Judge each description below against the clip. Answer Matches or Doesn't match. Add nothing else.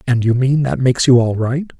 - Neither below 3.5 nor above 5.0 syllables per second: Doesn't match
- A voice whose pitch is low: Matches